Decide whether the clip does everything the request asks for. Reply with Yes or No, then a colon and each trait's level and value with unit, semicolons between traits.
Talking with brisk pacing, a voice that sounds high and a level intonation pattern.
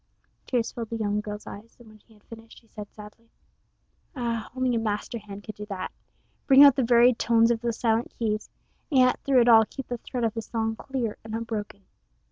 Yes: fast, 220 wpm; high, 225 Hz; narrow, 2.1 semitones